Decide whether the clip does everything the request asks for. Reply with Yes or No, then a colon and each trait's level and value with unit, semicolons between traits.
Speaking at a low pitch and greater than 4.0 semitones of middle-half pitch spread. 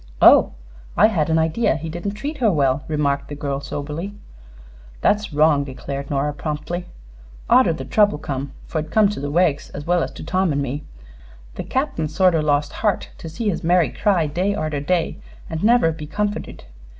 No: medium, 160 Hz; average, 4.7 semitones